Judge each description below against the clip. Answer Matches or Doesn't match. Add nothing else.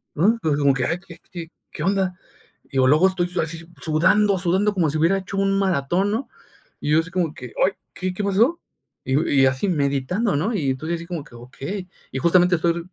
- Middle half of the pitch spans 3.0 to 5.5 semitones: Matches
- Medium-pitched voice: Matches